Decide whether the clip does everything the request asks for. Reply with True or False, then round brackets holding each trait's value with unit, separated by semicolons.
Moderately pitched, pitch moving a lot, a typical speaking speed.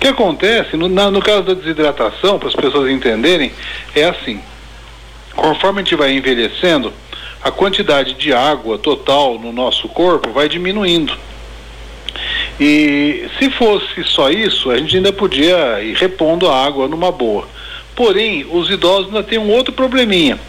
True (180 Hz; 7.5 semitones; 155 wpm)